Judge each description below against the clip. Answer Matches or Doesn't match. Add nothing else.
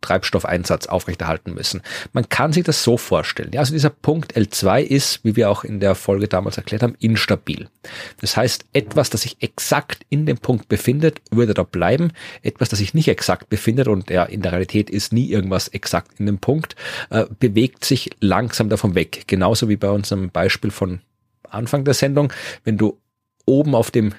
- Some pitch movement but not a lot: Matches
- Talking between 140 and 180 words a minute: Doesn't match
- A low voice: Matches